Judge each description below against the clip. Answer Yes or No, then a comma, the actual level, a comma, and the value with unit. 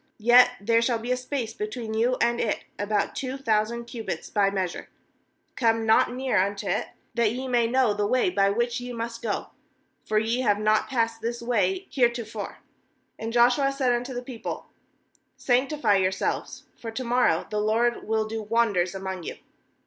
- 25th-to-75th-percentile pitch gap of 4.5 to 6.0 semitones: No, narrow, 2.4 semitones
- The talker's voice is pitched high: Yes, high, 230 Hz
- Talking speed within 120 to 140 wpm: No, average, 175 wpm